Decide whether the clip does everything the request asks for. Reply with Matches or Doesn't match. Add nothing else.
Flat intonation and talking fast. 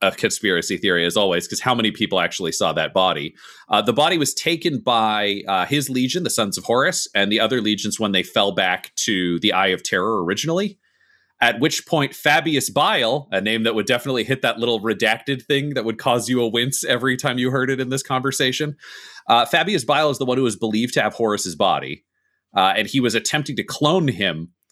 Doesn't match